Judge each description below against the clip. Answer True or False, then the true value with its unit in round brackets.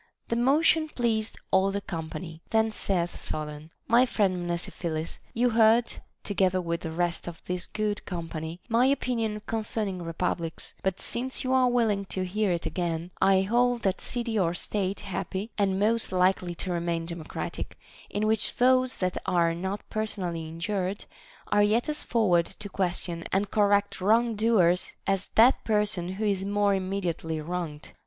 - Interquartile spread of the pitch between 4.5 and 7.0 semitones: False (4.1 semitones)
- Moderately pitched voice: False (195 Hz)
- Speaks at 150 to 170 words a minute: True (160 wpm)